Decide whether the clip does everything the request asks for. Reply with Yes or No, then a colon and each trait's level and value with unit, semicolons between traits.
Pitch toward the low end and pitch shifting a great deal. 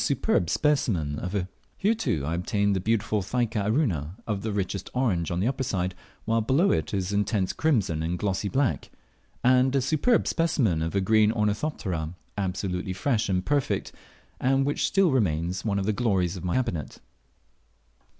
Yes: low, 105 Hz; wide, 5.7 semitones